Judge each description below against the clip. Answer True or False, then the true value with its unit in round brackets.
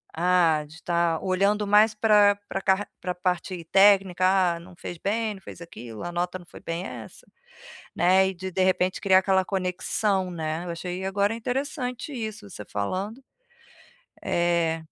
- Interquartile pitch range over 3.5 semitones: False (2.8 semitones)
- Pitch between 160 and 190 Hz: True (185 Hz)